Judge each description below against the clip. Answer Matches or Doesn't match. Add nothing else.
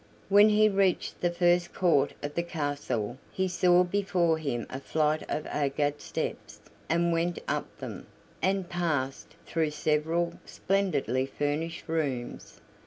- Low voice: Doesn't match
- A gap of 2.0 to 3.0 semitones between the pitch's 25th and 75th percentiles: Doesn't match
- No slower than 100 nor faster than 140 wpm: Matches